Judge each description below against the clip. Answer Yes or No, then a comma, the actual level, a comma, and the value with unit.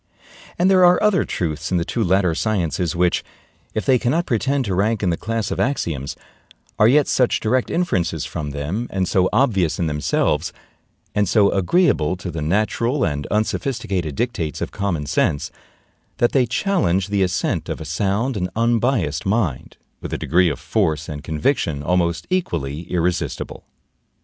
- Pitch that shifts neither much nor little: No, wide, 6.3 semitones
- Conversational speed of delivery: Yes, average, 165 wpm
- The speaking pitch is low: Yes, very low, 95 Hz